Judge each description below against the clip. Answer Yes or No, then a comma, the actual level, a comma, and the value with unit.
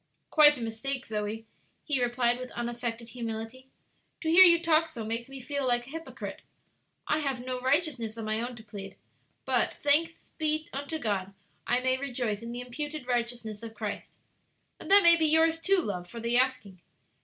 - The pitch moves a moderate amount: Yes, average, 4.6 semitones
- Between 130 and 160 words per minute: No, average, 185 wpm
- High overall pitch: Yes, very high, 250 Hz